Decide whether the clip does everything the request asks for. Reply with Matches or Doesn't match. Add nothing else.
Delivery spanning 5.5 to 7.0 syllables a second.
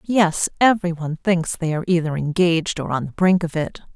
Matches